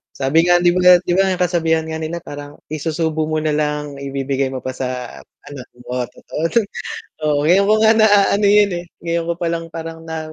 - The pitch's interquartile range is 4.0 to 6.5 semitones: No, average, 3.4 semitones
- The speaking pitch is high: No, medium, 160 Hz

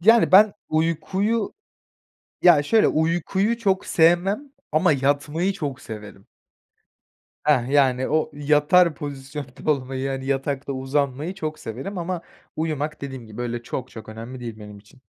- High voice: No, medium, 145 Hz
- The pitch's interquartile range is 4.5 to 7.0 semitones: Yes, average, 4.8 semitones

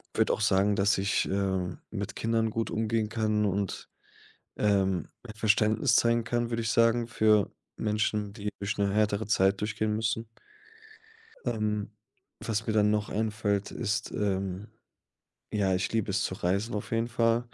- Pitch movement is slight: Yes, narrow, 1.9 semitones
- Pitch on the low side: Yes, low, 105 Hz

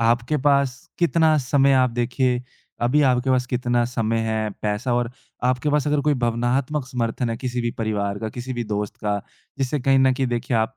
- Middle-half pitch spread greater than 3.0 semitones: No, narrow, 2.6 semitones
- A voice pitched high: No, low, 125 Hz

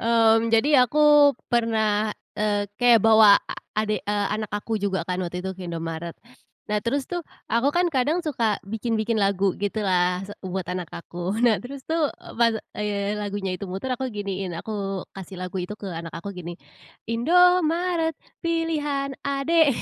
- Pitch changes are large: Yes, wide, 5.9 semitones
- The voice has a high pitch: Yes, high, 215 Hz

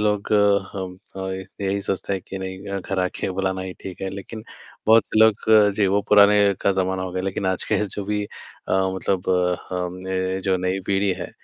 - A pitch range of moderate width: No, narrow, 1.2 semitones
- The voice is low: Yes, very low, 95 Hz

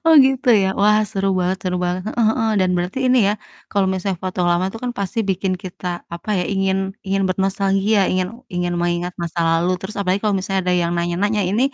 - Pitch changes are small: Yes, narrow, 2.2 semitones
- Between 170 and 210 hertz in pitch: Yes, high, 190 Hz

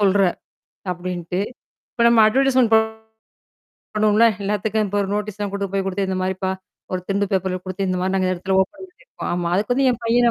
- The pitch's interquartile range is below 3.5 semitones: Yes, average, 2.9 semitones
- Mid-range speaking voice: No, high, 200 Hz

